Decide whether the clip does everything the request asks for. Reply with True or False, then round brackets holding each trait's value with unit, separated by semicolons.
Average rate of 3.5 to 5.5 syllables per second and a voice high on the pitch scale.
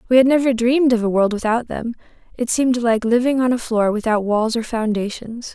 False (5.7 syllables/s; 235 Hz)